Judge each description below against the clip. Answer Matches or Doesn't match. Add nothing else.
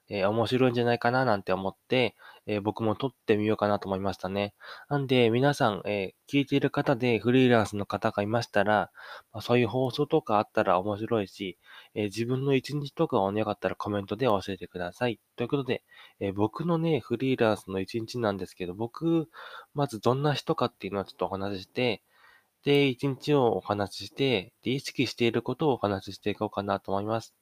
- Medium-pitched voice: Doesn't match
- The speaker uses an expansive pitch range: Doesn't match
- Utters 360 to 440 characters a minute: Matches